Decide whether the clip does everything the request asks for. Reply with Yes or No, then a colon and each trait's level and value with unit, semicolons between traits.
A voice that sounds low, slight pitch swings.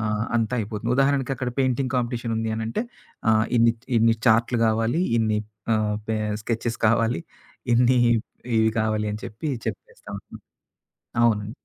Yes: low, 115 Hz; narrow, 1.8 semitones